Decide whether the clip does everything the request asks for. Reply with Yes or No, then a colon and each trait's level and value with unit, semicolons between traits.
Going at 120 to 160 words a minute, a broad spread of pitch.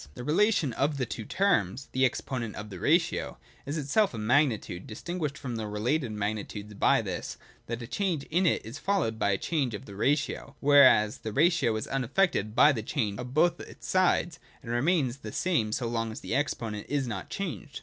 No: average, 200 wpm; wide, 5.9 semitones